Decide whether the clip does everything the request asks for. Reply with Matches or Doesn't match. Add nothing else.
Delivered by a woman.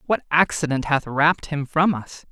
Doesn't match